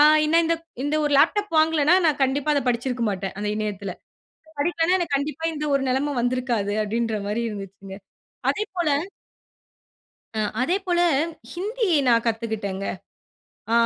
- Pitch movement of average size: No, wide, 6.9 semitones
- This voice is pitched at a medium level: No, very high, 265 Hz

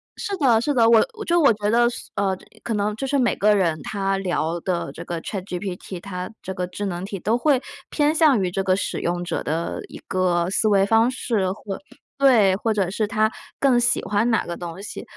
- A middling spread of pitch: Yes, average, 4.1 semitones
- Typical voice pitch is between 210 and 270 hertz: No, high, 200 Hz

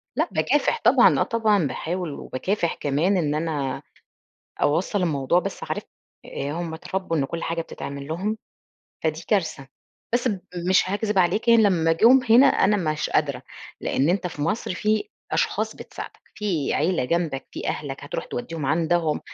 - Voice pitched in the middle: Yes, medium, 170 Hz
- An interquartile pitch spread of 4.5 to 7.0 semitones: Yes, average, 4.8 semitones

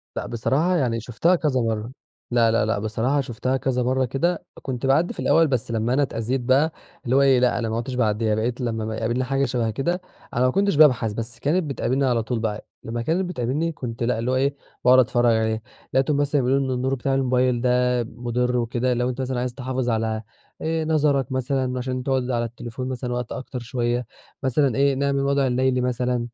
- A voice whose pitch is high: No, low, 125 Hz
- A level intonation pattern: Yes, narrow, 2.3 semitones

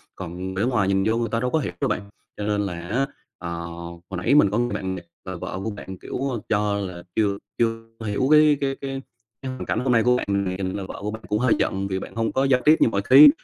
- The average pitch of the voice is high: No, low, 105 Hz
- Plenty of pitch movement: No, average, 4.7 semitones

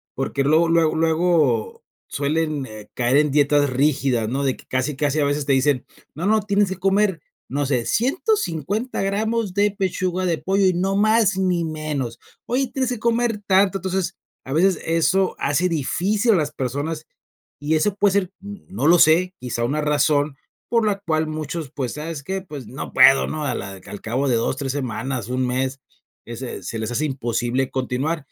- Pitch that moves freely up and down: Yes, wide, 6.1 semitones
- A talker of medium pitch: Yes, medium, 155 Hz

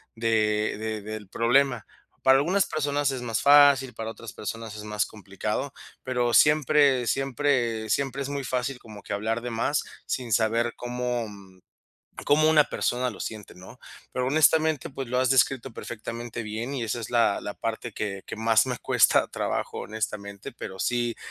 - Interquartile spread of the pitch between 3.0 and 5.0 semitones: Yes, average, 3.7 semitones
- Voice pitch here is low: Yes, low, 120 Hz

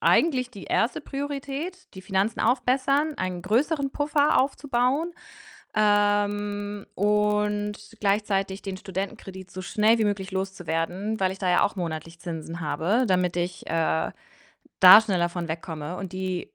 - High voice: Yes, high, 205 Hz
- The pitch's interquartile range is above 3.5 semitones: Yes, average, 4.3 semitones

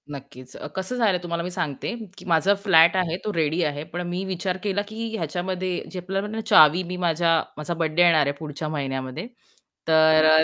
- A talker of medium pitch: Yes, medium, 170 Hz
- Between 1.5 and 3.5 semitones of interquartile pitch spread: Yes, average, 3.1 semitones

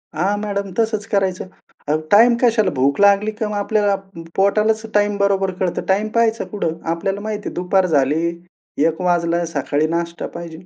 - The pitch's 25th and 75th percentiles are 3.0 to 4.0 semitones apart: Yes, average, 3.7 semitones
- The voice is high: Yes, high, 195 Hz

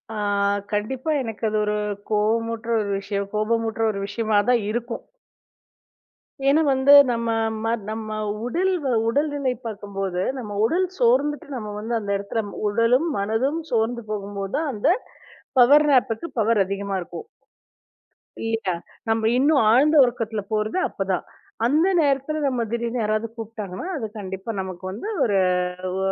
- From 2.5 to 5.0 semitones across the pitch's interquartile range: Yes, average, 3.8 semitones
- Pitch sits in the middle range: No, high, 225 Hz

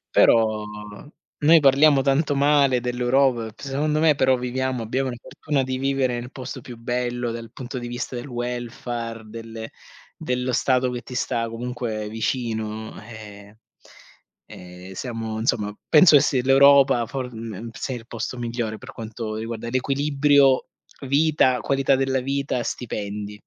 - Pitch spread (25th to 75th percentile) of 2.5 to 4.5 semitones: Yes, average, 2.9 semitones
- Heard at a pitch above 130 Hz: No, low, 125 Hz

